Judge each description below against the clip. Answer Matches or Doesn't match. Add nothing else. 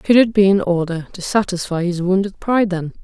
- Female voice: Matches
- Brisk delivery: Matches